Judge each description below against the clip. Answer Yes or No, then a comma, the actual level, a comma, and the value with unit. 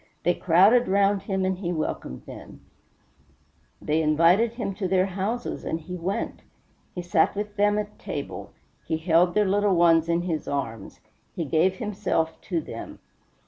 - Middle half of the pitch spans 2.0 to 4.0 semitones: Yes, average, 3.5 semitones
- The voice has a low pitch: No, medium, 185 Hz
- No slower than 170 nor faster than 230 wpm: No, average, 160 wpm